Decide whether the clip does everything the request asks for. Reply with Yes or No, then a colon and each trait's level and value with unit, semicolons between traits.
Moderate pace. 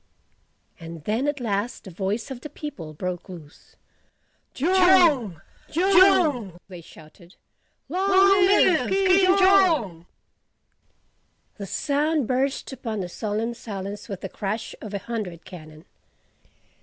No: slow, 120 wpm